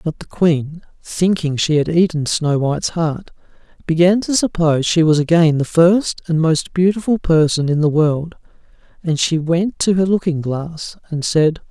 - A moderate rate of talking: Yes, average, 175 wpm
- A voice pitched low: No, medium, 165 Hz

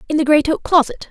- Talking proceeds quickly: Yes, fast, 270 wpm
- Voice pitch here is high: Yes, very high, 295 Hz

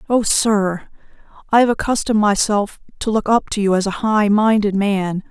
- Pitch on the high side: Yes, high, 210 Hz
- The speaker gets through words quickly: No, average, 180 wpm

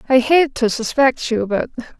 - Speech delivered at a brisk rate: No, average, 180 wpm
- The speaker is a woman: Yes, female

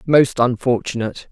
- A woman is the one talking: Yes, female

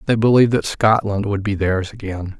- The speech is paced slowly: No, average, 200 wpm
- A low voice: Yes, low, 105 Hz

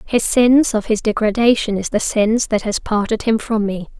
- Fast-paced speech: Yes, fast, 210 wpm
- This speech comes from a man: No, female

